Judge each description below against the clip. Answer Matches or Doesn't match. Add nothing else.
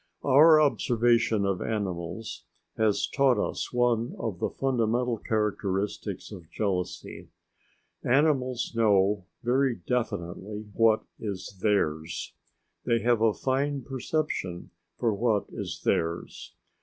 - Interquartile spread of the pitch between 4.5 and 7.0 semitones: Doesn't match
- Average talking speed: Doesn't match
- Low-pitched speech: Matches